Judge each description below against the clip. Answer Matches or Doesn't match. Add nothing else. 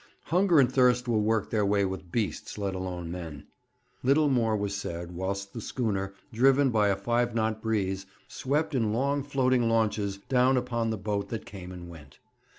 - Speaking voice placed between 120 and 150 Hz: Doesn't match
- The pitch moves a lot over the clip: Doesn't match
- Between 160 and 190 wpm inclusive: Matches